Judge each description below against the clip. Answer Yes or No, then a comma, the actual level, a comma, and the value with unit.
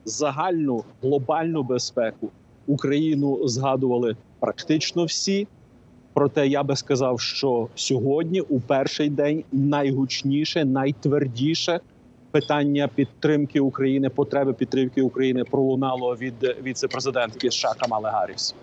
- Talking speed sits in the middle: No, slow, 95 wpm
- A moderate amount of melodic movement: No, narrow, 2.2 semitones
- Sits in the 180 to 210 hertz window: No, medium, 140 Hz